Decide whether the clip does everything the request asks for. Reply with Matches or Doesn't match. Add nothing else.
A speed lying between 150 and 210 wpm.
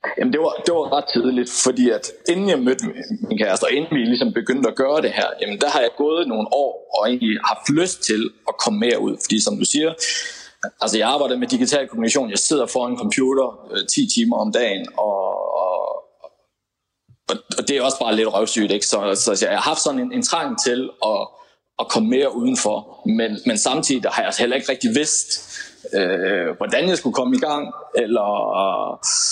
Matches